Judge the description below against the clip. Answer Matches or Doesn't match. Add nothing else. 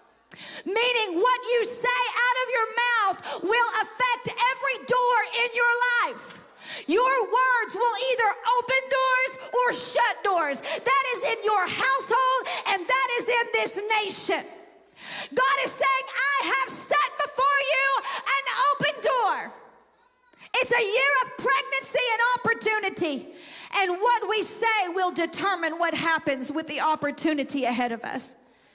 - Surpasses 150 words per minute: Doesn't match